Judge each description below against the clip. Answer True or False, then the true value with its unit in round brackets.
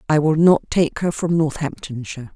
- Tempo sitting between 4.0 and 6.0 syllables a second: True (5.1 syllables/s)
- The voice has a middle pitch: True (155 Hz)